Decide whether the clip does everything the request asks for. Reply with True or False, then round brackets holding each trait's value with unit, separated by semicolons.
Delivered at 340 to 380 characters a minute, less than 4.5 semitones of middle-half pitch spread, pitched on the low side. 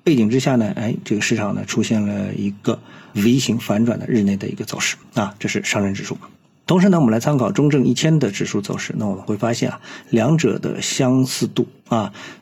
False (320 characters per minute; 4.1 semitones; 120 Hz)